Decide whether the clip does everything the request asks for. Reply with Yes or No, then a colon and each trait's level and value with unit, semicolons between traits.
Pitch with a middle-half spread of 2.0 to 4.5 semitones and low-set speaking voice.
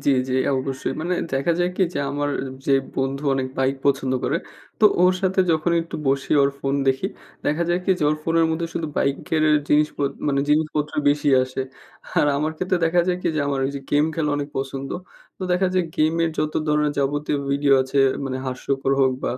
No: average, 3.1 semitones; medium, 145 Hz